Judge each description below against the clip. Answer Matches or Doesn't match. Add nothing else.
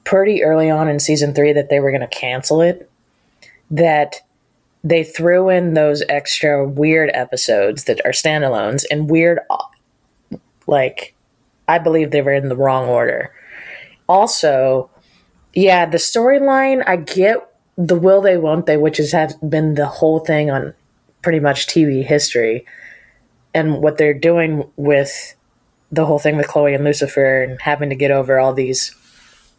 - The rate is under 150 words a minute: Doesn't match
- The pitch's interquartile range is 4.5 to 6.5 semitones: Doesn't match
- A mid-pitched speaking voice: Matches